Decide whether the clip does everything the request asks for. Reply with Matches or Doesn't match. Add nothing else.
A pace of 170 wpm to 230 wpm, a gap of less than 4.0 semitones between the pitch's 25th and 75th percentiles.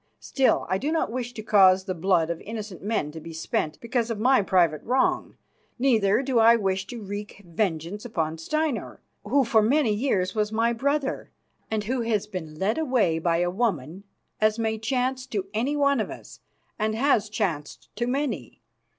Doesn't match